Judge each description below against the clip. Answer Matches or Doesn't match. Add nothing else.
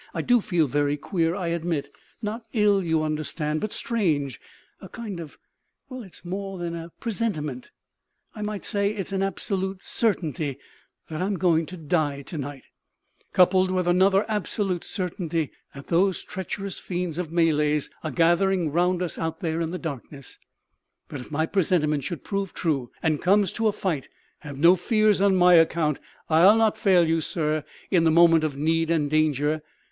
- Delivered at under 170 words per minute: Doesn't match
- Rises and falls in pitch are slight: Doesn't match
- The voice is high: Doesn't match